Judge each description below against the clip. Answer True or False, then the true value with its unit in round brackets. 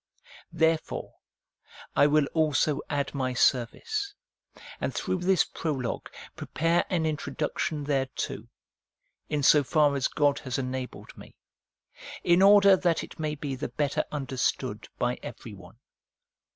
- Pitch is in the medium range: True (150 Hz)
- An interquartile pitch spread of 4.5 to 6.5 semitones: False (3.3 semitones)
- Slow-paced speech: True (125 wpm)